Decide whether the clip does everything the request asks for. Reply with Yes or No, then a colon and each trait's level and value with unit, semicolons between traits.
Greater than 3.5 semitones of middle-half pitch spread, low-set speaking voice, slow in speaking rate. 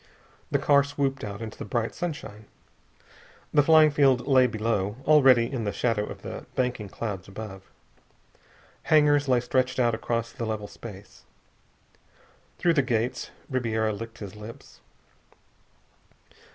Yes: average, 3.9 semitones; low, 115 Hz; slow, 130 wpm